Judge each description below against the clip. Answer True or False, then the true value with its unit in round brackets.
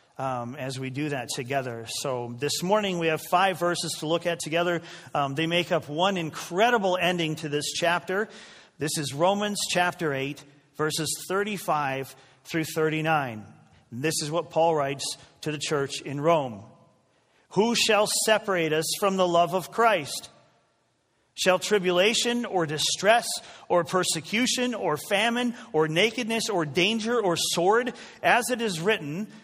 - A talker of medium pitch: True (170 Hz)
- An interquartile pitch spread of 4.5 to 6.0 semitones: True (5.0 semitones)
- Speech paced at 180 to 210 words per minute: False (150 wpm)